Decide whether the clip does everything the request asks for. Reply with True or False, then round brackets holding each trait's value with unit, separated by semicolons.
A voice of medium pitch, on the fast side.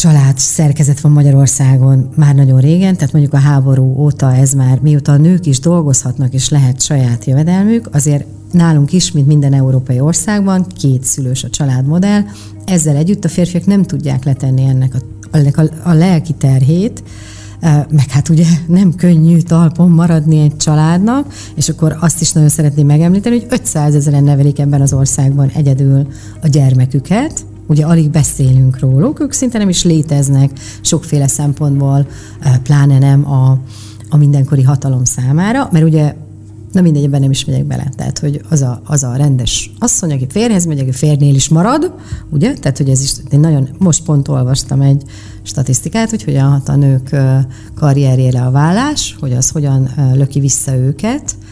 True (145 Hz; 165 wpm)